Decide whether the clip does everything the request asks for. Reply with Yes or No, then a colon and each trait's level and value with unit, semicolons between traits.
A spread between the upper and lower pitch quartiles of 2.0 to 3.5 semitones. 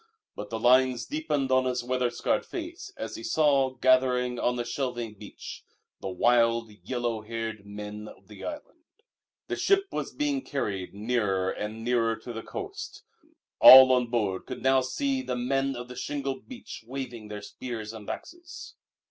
Yes: average, 3.1 semitones